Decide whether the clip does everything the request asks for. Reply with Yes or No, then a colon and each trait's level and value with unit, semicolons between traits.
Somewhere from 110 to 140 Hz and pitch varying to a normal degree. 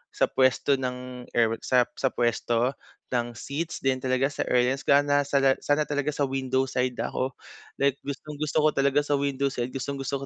No: low, 135 Hz; narrow, 2.0 semitones